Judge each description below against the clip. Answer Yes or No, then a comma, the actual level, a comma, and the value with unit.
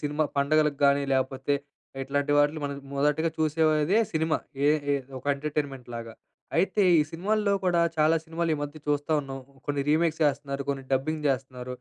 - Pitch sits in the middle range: Yes, medium, 145 Hz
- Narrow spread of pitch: Yes, narrow, 2.3 semitones